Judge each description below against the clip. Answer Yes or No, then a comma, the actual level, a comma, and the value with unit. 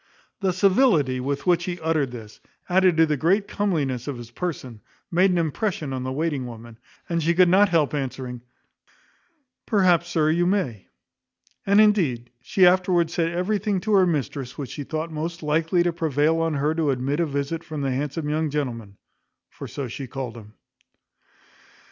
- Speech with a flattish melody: No, average, 4.7 semitones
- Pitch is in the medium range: Yes, medium, 160 Hz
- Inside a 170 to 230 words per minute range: Yes, average, 175 wpm